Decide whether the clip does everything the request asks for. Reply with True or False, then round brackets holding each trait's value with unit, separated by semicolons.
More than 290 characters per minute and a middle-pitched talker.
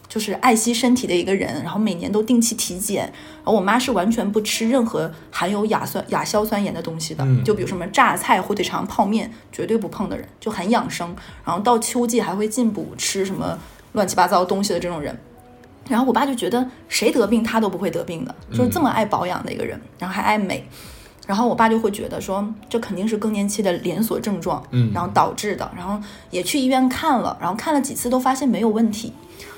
False (335 characters per minute; 215 Hz)